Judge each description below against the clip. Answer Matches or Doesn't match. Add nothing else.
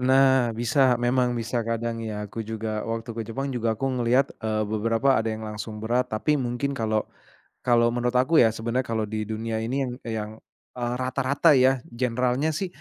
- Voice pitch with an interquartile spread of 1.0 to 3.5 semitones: Matches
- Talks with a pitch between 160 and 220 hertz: Doesn't match